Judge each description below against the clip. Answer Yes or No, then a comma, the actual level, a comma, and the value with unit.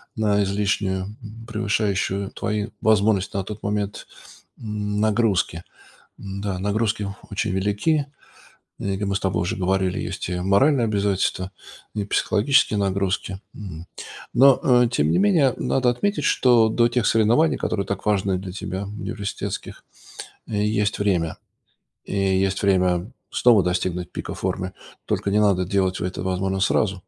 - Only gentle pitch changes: Yes, narrow, 2.3 semitones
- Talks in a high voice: No, low, 100 Hz